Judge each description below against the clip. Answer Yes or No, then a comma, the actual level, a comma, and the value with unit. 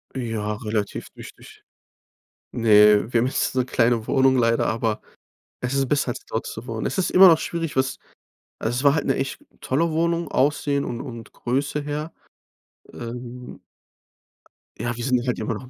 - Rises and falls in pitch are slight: No, average, 3.6 semitones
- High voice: No, low, 125 Hz